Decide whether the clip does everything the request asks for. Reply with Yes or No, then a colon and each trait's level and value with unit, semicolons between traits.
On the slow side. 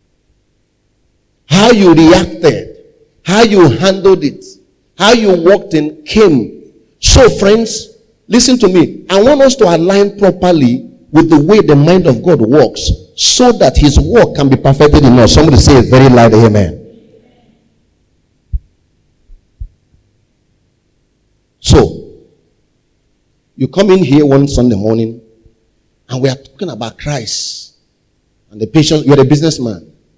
Yes: slow, 130 wpm